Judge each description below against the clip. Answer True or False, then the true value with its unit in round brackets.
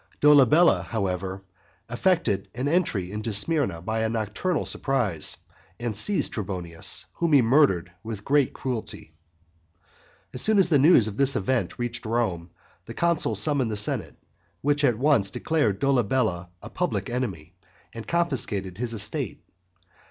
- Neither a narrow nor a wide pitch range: False (6.2 semitones)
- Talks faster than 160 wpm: False (140 wpm)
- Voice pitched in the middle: False (115 Hz)